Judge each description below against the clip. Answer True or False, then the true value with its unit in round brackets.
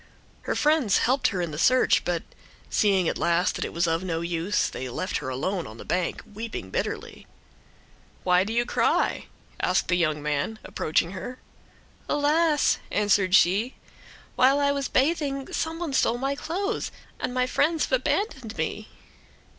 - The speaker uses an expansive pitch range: True (8.3 semitones)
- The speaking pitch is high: True (215 Hz)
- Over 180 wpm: False (165 wpm)